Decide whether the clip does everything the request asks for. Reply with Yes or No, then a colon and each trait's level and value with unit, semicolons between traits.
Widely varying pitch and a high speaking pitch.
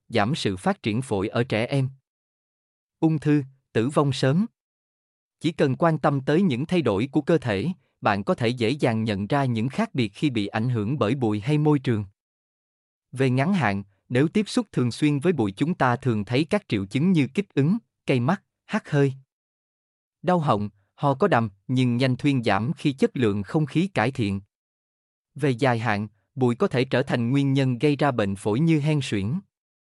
No: wide, 5.8 semitones; low, 130 Hz